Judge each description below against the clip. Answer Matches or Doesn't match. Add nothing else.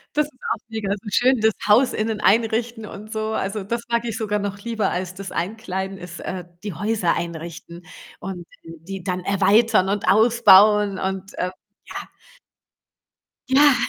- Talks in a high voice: Matches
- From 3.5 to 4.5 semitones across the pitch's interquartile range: Doesn't match